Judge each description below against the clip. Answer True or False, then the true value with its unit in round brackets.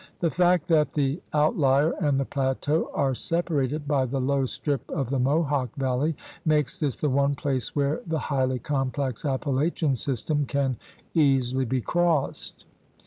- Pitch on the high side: False (140 Hz)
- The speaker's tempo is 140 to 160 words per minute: True (155 wpm)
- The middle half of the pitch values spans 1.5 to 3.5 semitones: True (2.4 semitones)